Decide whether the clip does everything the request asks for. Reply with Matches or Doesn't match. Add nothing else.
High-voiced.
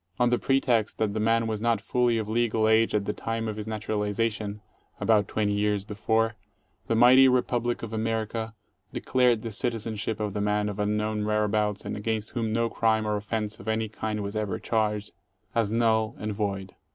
Doesn't match